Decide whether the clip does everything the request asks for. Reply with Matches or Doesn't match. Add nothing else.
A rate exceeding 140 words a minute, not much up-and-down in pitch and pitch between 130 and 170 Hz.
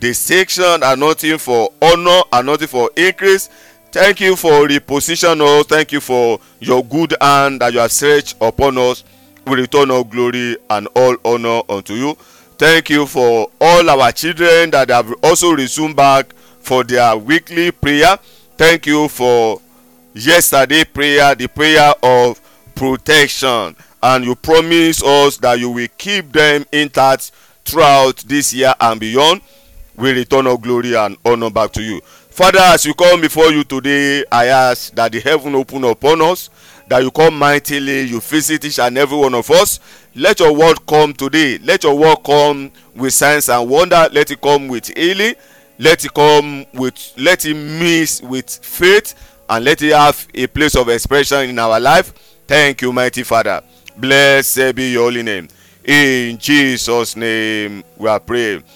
Doesn't match